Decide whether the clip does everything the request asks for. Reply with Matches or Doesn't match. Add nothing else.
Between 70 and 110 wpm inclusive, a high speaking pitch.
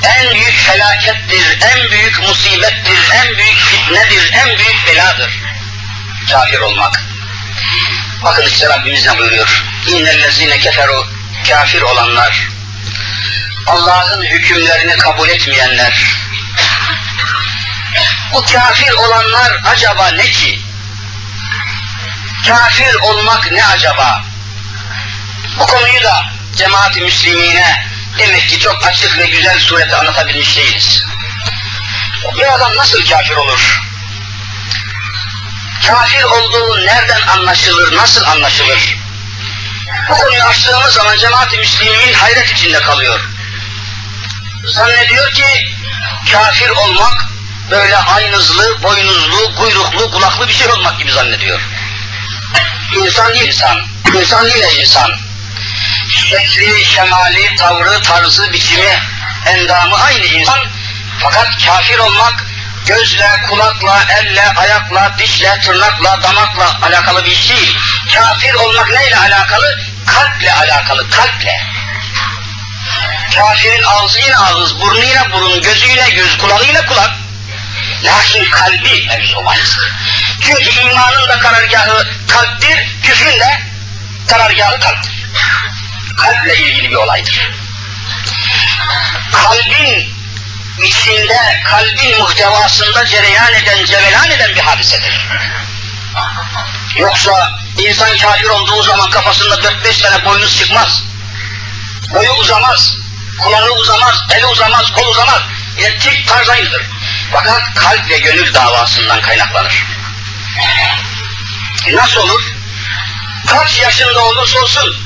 Doesn't match